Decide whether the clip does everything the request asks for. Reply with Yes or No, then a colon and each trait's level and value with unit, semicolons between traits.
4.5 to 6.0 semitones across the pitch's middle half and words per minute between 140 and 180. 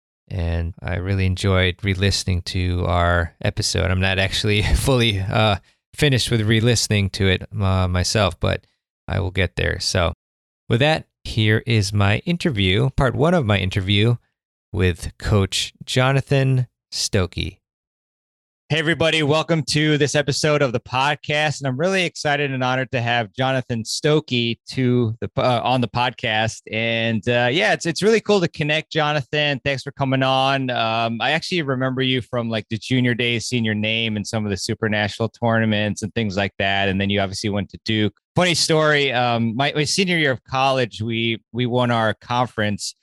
Yes: average, 5.1 semitones; average, 175 wpm